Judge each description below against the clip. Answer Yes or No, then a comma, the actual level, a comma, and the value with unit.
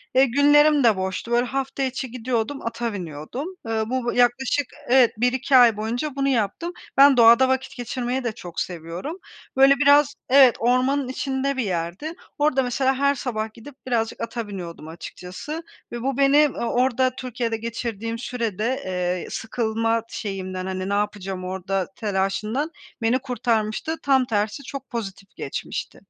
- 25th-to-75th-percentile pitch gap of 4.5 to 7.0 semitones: No, average, 4.1 semitones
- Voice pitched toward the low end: No, high, 240 Hz